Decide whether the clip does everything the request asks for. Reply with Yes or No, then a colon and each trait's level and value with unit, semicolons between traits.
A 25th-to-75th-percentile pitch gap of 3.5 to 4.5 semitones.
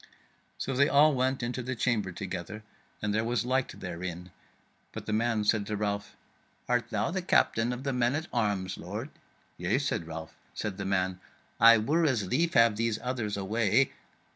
Yes: average, 4.0 semitones